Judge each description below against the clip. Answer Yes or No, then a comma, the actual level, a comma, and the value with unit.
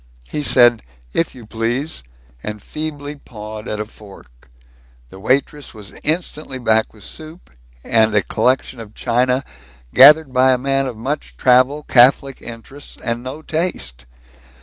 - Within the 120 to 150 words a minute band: Yes, average, 145 wpm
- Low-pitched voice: Yes, low, 125 Hz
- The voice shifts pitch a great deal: No, average, 4.4 semitones